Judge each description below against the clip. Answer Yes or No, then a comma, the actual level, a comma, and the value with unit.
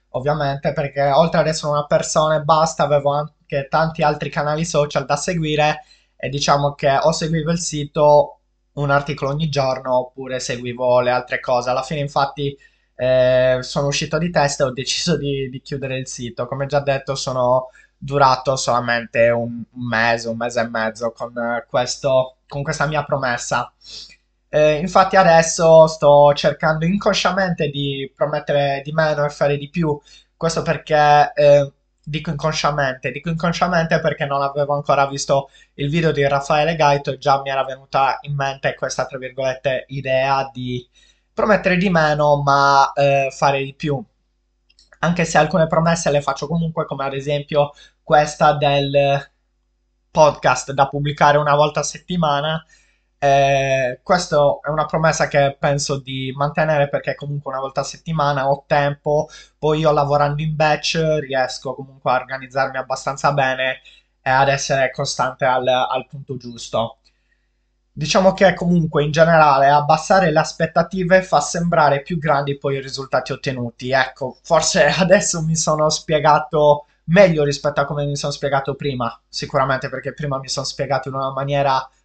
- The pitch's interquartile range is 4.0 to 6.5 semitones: No, narrow, 2.5 semitones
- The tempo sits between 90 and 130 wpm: No, average, 155 wpm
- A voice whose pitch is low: No, medium, 145 Hz